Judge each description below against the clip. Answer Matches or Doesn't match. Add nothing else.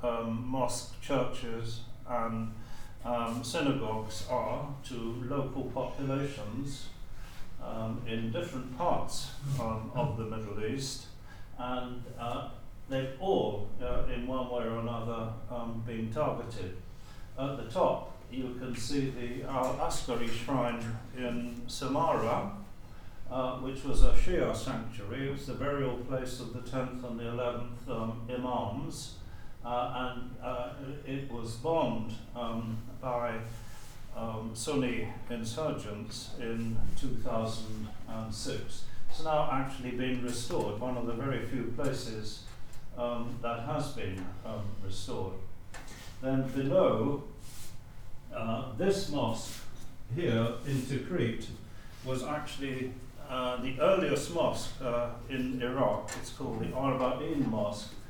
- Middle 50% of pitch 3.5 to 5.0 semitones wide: Doesn't match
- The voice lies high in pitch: Doesn't match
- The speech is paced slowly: Matches